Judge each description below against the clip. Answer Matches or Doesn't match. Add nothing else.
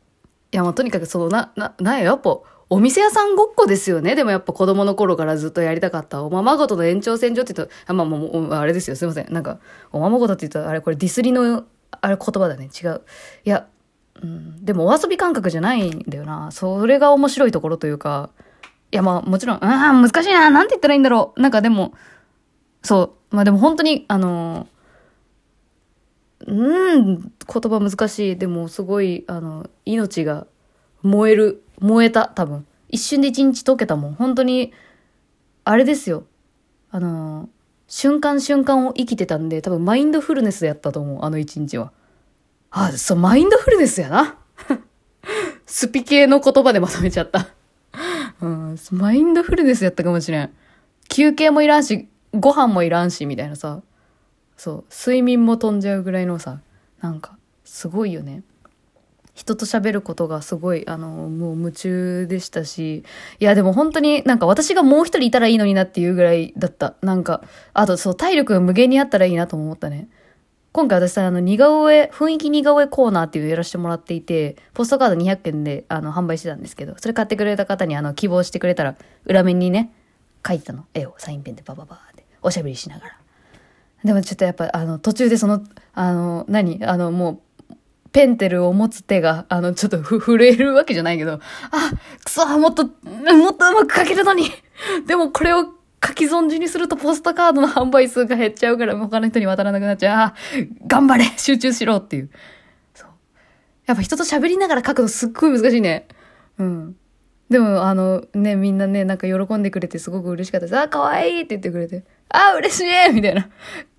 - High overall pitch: Matches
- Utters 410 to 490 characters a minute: Doesn't match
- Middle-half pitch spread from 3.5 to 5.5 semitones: Doesn't match